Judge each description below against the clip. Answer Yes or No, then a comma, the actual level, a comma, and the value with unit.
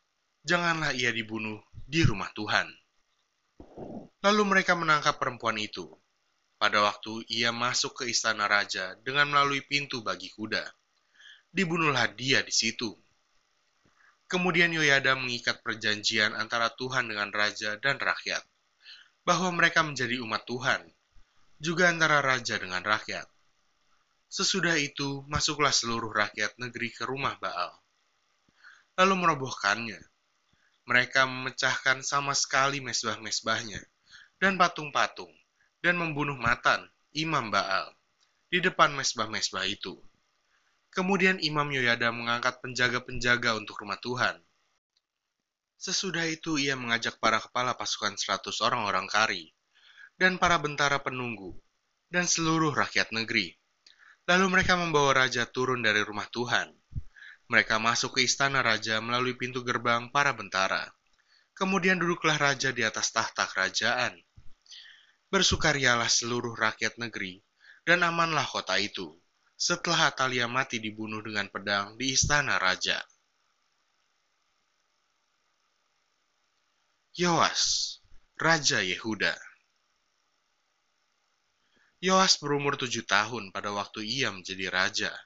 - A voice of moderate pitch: No, low, 130 Hz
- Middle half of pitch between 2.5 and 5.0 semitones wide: No, wide, 5.5 semitones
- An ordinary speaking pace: Yes, average, 110 wpm